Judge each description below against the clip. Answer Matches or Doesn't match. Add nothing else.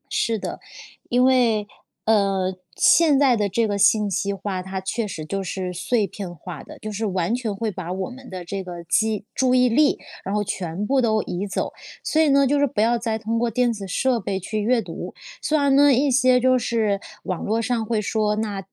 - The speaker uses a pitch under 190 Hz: Doesn't match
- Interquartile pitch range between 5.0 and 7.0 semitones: Doesn't match